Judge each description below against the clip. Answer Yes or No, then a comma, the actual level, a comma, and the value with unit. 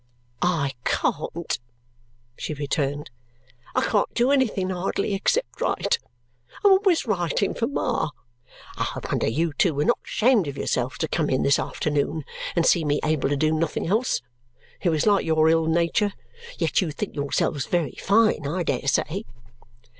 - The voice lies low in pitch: No, medium, 165 Hz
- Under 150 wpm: No, average, 160 wpm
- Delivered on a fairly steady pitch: No, wide, 5.5 semitones